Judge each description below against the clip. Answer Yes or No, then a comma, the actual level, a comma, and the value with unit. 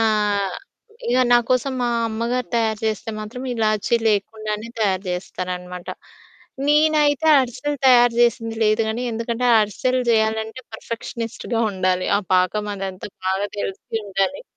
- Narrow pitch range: No, average, 3.1 semitones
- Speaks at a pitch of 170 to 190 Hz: No, high, 220 Hz